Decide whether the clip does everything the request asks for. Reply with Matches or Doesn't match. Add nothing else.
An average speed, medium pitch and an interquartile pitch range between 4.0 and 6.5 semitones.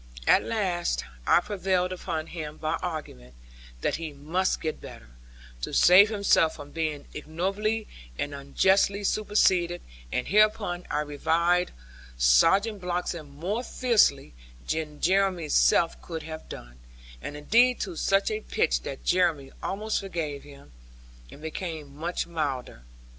Doesn't match